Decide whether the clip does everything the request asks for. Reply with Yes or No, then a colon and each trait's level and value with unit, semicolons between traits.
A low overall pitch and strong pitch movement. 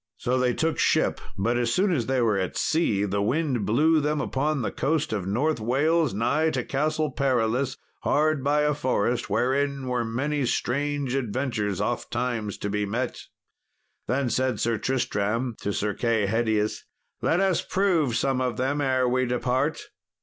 No: low, 130 Hz; average, 4.1 semitones